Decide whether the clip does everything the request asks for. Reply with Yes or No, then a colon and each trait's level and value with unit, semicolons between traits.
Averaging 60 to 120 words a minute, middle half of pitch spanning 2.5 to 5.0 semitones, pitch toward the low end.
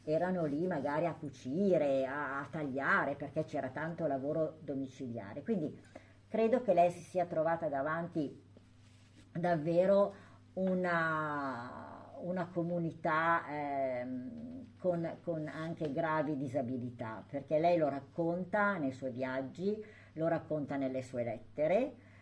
No: slow, 115 wpm; average, 4.2 semitones; medium, 155 Hz